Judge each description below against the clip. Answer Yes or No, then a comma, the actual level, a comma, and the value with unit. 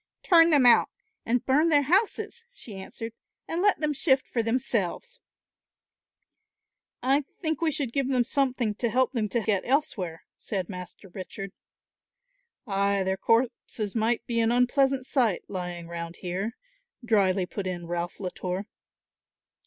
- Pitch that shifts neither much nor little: No, wide, 6.0 semitones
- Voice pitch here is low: No, high, 230 Hz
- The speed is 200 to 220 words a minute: No, average, 145 wpm